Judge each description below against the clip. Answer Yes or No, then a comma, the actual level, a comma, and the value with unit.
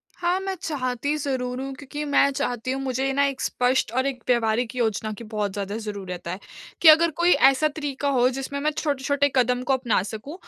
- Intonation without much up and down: No, average, 3.2 semitones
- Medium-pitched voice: No, very high, 260 Hz